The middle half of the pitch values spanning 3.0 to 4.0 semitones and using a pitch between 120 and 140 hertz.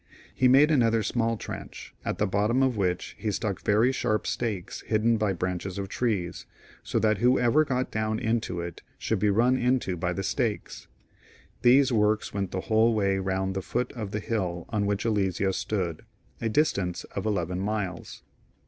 No: average, 3.5 semitones; low, 105 Hz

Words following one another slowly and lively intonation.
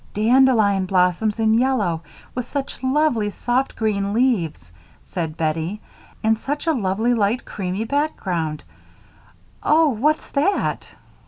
Yes: slow, 115 wpm; wide, 5.7 semitones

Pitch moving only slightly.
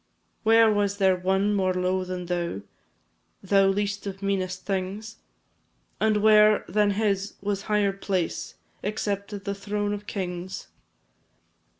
Yes: narrow, 1.7 semitones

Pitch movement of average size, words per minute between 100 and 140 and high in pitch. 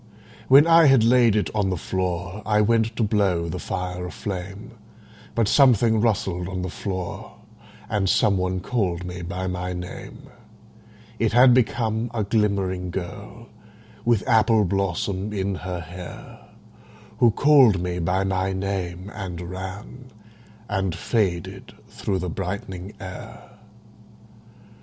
No: average, 3.4 semitones; slow, 135 wpm; very low, 95 Hz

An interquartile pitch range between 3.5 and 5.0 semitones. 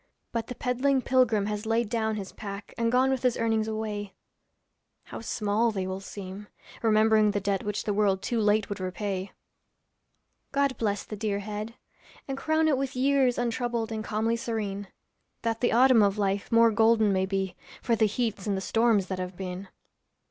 No: narrow, 2.6 semitones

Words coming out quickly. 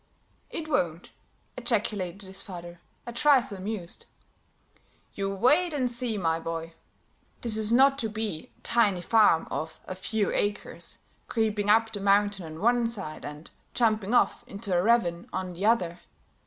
No: average, 155 wpm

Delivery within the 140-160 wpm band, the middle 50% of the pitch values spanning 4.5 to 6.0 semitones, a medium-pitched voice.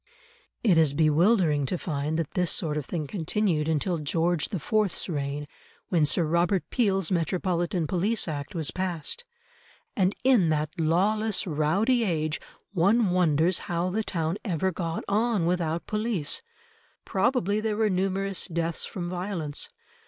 No: average, 145 wpm; average, 3.8 semitones; medium, 175 Hz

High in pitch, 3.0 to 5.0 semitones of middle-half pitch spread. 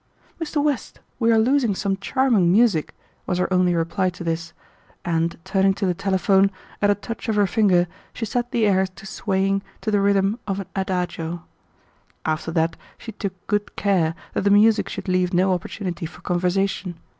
No: high, 195 Hz; narrow, 2.6 semitones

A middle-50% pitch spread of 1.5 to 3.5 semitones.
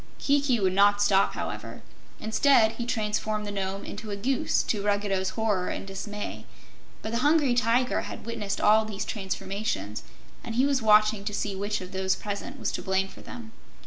Yes: average, 2.7 semitones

